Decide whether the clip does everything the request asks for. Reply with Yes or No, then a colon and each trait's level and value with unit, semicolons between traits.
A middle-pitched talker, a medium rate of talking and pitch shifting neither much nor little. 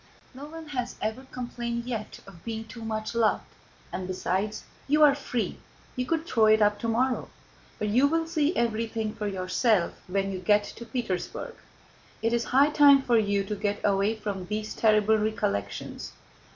No: high, 220 Hz; average, 170 wpm; average, 3.5 semitones